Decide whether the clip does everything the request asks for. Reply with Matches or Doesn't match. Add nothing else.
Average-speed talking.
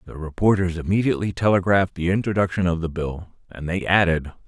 Matches